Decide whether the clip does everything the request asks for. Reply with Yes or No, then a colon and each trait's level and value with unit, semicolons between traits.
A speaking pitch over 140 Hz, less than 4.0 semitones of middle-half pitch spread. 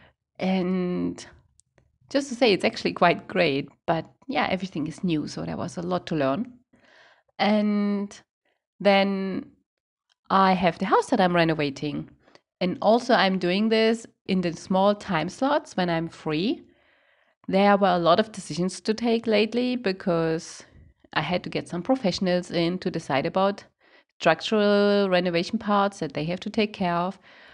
No: high, 190 Hz; average, 4.3 semitones